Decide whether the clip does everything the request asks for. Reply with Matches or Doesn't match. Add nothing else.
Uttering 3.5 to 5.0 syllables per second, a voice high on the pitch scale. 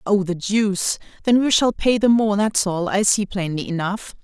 Matches